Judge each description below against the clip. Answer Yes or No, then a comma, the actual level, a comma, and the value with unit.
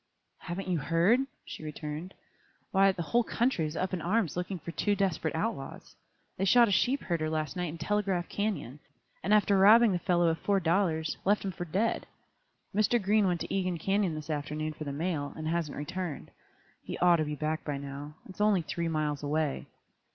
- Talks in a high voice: No, medium, 175 Hz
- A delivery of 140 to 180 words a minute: No, average, 200 wpm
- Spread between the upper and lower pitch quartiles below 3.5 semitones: No, average, 4.0 semitones